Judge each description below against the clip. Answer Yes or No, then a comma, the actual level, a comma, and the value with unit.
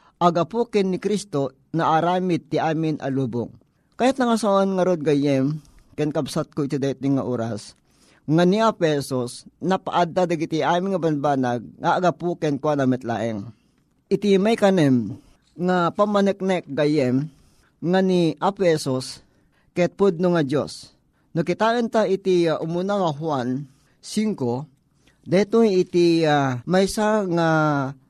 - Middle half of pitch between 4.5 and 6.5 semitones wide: Yes, average, 5.1 semitones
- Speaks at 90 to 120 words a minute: No, average, 130 wpm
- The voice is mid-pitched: Yes, medium, 160 Hz